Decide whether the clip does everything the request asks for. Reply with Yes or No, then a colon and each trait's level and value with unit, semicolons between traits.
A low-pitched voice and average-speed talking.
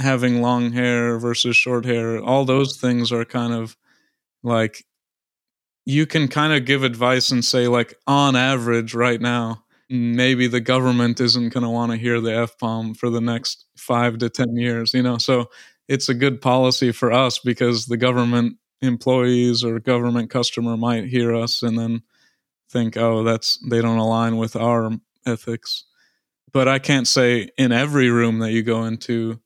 Yes: low, 120 Hz; average, 175 wpm